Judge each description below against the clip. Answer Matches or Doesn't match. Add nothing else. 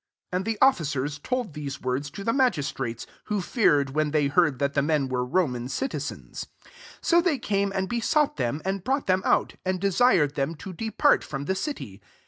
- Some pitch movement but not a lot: Doesn't match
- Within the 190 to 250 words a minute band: Matches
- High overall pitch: Doesn't match